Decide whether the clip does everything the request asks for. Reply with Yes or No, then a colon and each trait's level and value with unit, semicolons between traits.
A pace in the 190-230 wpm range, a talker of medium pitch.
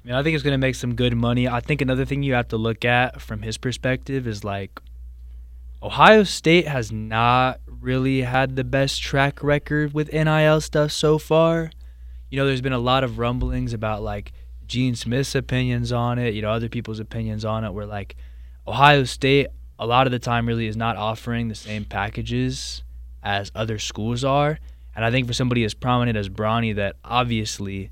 No: average, 200 wpm; low, 120 Hz